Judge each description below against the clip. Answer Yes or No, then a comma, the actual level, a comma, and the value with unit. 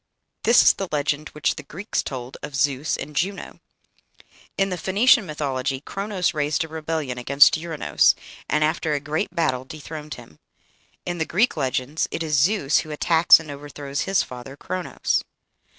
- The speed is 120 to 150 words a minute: No, average, 165 wpm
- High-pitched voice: No, medium, 150 Hz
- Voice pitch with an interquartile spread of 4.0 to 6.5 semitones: No, average, 3.3 semitones